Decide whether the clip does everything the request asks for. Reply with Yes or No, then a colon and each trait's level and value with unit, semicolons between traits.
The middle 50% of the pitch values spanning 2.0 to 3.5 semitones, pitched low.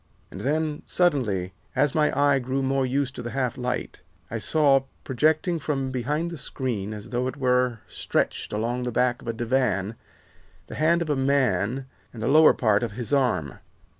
Yes: average, 3.2 semitones; low, 130 Hz